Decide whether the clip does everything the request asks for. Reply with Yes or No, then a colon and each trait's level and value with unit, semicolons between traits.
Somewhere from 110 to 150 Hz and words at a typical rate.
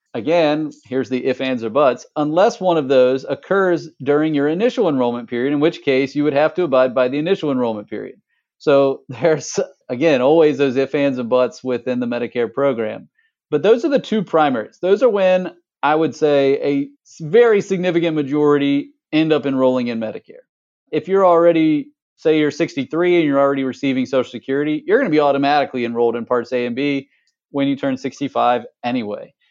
Yes: medium, 140 Hz; average, 185 wpm